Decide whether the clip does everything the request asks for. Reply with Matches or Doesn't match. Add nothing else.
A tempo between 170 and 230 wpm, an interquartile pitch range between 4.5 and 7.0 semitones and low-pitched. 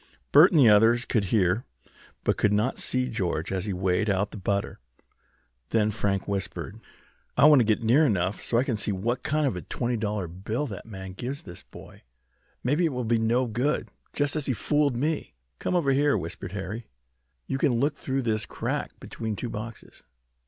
Matches